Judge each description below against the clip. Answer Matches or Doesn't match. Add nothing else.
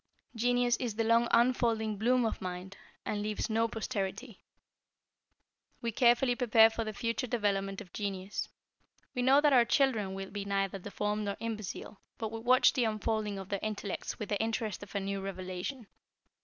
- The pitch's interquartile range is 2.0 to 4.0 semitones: Matches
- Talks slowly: Doesn't match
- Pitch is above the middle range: Matches